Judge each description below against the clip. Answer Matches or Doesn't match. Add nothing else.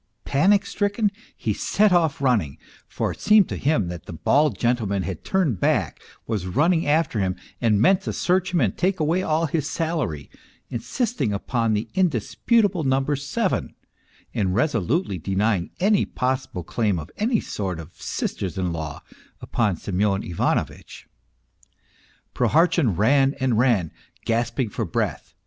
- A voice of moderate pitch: Doesn't match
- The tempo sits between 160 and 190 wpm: Doesn't match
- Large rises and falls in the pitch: Matches